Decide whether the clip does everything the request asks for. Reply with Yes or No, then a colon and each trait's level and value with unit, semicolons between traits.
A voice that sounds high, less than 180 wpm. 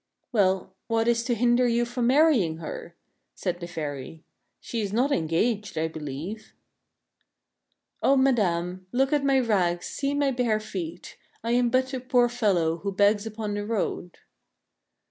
Yes: high, 215 Hz; average, 165 wpm